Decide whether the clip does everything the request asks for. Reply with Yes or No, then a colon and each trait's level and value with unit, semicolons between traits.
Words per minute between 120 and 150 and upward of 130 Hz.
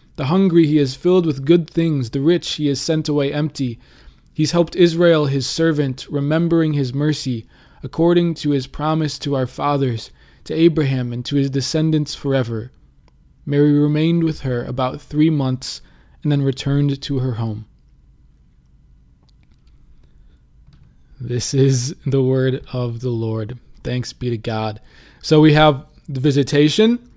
Yes: average, 145 wpm; medium, 140 Hz